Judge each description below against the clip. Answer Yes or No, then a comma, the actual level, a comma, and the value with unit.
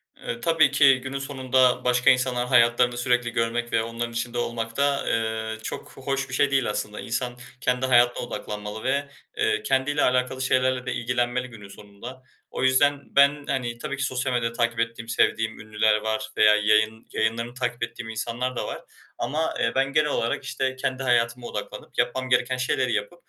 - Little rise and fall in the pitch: Yes, narrow, 2.3 semitones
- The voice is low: Yes, low, 125 Hz